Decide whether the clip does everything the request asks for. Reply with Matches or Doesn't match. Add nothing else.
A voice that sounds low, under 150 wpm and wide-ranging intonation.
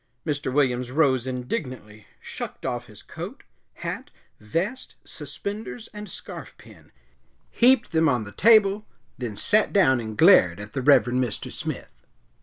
Matches